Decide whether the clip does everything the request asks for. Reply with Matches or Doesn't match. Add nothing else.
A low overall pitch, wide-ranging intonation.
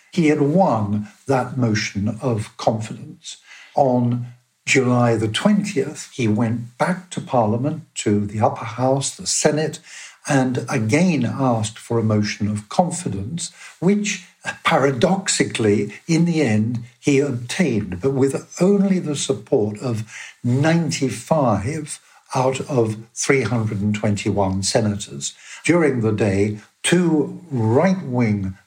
Matches